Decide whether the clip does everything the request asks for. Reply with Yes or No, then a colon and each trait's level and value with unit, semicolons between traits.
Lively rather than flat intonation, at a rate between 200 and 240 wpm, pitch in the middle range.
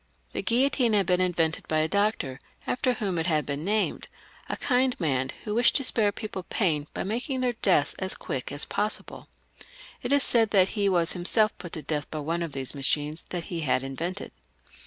Yes: wide, 5.8 semitones; fast, 205 wpm; medium, 180 Hz